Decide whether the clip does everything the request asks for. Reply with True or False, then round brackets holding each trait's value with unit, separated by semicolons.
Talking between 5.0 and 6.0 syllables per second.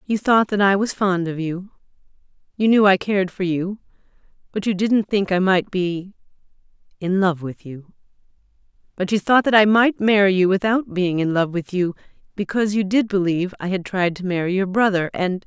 True (5.2 syllables/s)